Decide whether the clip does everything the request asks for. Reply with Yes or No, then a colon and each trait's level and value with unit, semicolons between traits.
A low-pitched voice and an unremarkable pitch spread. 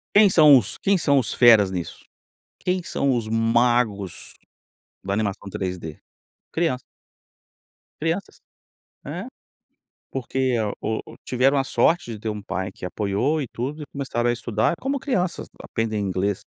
No: low, 120 Hz; wide, 5.9 semitones